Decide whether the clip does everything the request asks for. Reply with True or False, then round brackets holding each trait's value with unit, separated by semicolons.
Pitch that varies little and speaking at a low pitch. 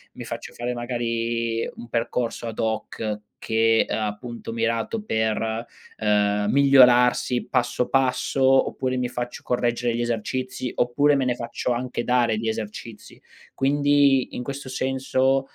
True (2.3 semitones; 120 Hz)